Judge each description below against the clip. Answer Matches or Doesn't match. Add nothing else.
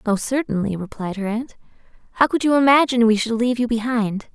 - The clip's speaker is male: Doesn't match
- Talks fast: Doesn't match